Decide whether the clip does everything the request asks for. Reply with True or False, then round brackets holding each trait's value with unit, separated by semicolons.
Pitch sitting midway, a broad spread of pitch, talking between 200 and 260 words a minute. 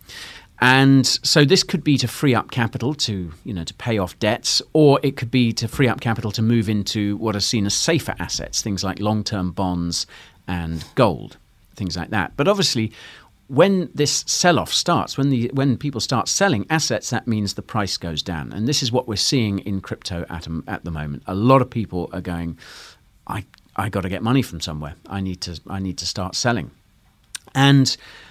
False (110 Hz; 6.3 semitones; 205 wpm)